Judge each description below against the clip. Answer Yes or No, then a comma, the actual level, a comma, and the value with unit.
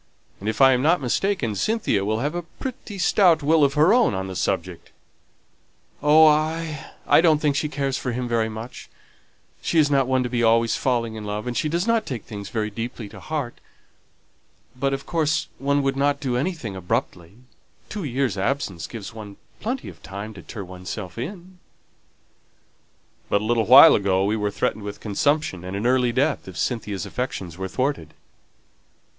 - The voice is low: Yes, low, 125 Hz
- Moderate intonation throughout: No, wide, 6.3 semitones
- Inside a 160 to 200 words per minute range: Yes, average, 185 wpm